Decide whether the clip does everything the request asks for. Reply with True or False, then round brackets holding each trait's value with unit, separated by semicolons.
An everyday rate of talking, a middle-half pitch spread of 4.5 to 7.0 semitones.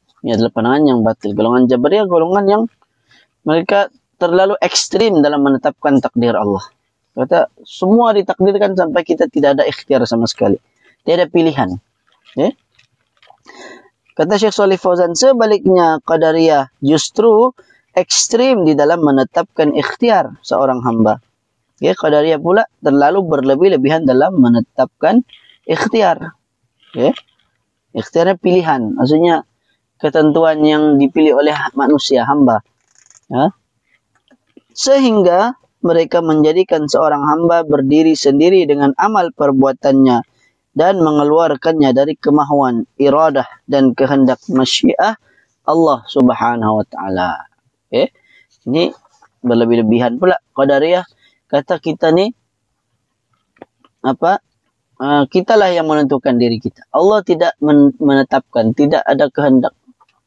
True (105 wpm; 5.4 semitones)